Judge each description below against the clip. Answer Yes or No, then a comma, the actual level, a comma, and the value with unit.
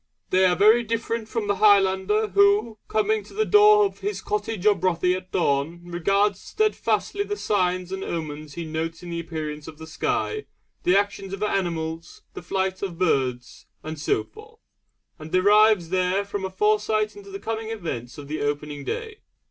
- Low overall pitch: No, high, 190 Hz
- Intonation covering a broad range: No, average, 4.6 semitones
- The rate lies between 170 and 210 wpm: Yes, average, 180 wpm